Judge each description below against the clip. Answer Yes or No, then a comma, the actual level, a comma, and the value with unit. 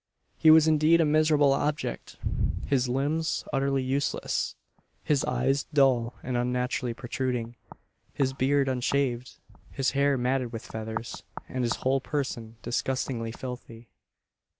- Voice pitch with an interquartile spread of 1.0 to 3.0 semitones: Yes, narrow, 2.5 semitones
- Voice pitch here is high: No, low, 130 Hz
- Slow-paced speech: Yes, slow, 125 wpm